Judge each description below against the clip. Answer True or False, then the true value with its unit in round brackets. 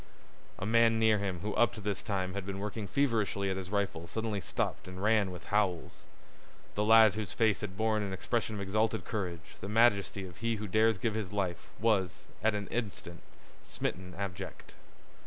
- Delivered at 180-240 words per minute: True (190 wpm)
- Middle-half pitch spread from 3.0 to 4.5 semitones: False (2.6 semitones)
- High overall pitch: False (105 Hz)